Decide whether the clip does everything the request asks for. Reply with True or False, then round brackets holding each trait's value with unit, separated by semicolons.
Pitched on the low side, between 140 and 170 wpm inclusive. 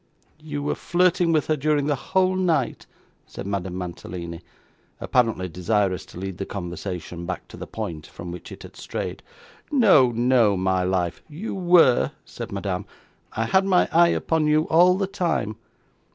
True (125 Hz; 165 wpm)